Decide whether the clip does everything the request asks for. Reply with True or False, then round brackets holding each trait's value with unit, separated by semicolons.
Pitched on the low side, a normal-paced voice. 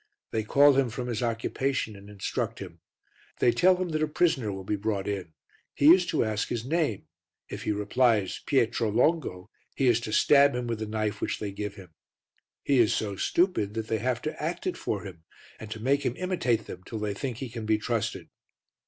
False (115 Hz; 215 wpm)